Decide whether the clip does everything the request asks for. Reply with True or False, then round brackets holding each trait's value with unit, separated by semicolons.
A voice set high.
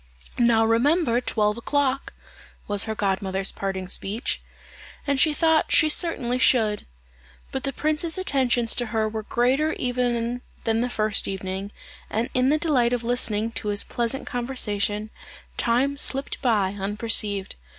True (235 Hz)